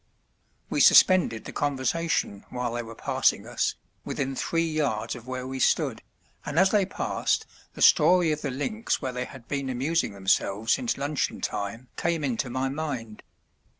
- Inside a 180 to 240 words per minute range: No, average, 165 wpm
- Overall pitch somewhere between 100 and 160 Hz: Yes, low, 135 Hz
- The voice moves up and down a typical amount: Yes, average, 4.7 semitones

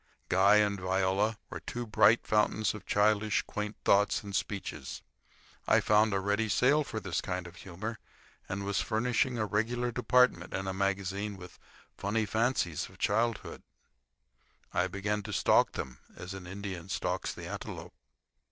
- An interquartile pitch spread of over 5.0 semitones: No, narrow, 2.4 semitones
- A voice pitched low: Yes, low, 105 Hz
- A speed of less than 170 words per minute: Yes, average, 155 wpm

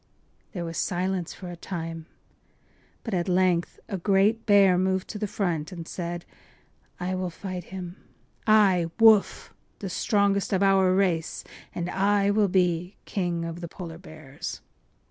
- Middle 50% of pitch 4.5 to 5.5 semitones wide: No, narrow, 2.4 semitones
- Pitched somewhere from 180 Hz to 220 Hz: Yes, medium, 185 Hz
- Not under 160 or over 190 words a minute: No, average, 145 wpm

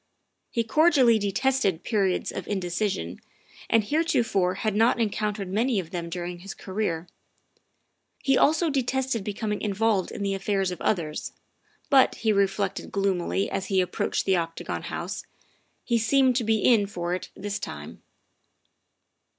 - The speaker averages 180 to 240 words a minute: No, average, 145 wpm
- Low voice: No, high, 205 Hz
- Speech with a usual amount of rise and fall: Yes, average, 3.7 semitones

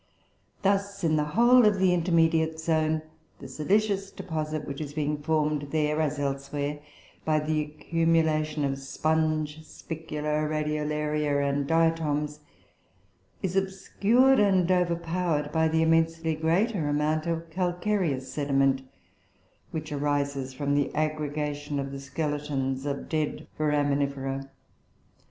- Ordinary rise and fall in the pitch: No, narrow, 2.1 semitones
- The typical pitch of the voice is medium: Yes, medium, 155 Hz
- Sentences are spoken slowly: Yes, slow, 120 wpm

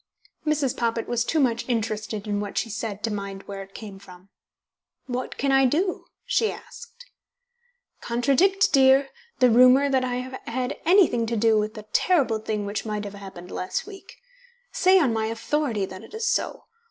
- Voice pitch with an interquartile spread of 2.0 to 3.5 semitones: No, average, 4.9 semitones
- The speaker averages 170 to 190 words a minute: Yes, average, 180 wpm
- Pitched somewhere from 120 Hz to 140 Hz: No, high, 235 Hz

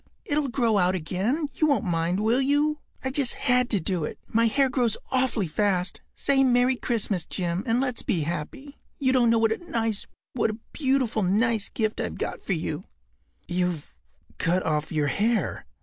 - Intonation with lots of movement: Yes, wide, 6.2 semitones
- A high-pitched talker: Yes, high, 225 Hz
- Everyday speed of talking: Yes, average, 175 wpm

